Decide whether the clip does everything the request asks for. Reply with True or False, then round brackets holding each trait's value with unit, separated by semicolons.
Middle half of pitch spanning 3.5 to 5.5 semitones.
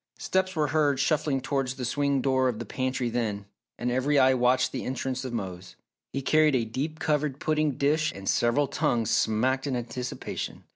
False (3.0 semitones)